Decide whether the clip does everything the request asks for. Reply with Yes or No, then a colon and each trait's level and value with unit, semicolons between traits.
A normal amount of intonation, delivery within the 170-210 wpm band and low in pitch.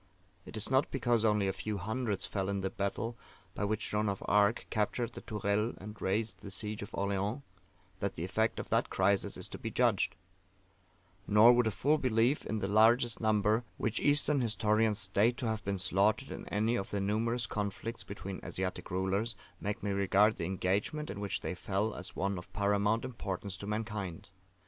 No: narrow, 2.3 semitones; average, 190 wpm; low, 105 Hz